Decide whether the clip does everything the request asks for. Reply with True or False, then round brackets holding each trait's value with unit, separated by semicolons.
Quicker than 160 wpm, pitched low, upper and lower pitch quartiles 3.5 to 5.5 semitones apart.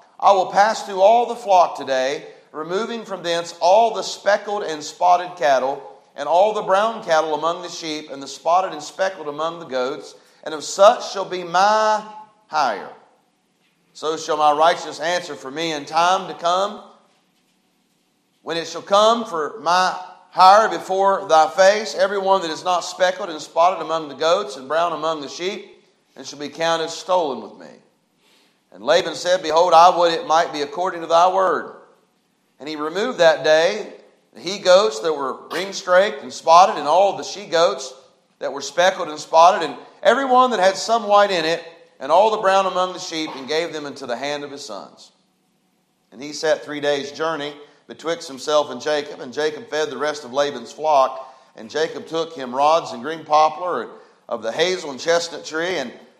False (190 wpm; 170 Hz; 4.1 semitones)